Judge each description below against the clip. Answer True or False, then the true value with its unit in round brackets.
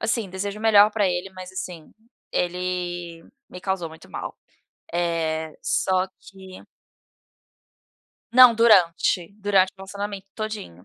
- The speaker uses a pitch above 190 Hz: False (185 Hz)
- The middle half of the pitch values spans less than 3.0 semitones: True (2.6 semitones)